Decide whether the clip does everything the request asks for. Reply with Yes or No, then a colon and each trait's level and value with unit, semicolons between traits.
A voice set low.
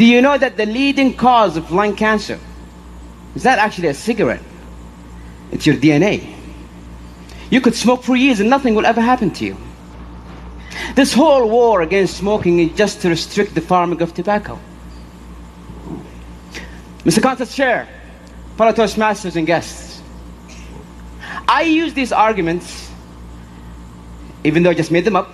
No: medium, 160 Hz